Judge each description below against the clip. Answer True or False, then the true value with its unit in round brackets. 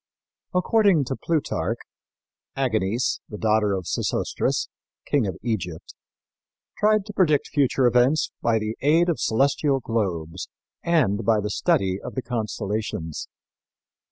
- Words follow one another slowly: True (125 wpm)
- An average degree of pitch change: False (5.9 semitones)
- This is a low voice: True (115 Hz)